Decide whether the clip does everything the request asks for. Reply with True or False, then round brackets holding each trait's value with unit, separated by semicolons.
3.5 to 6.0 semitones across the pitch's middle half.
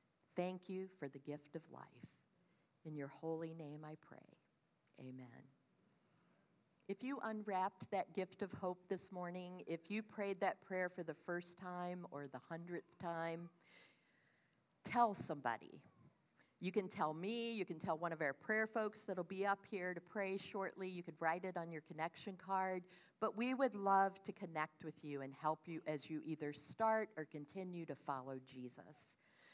True (3.8 semitones)